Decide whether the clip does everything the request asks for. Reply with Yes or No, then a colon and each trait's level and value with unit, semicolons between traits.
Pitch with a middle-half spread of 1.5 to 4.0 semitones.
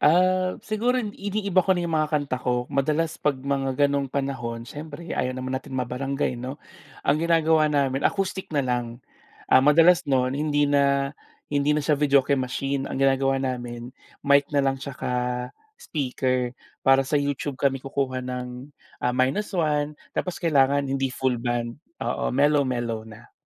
Yes: average, 2.7 semitones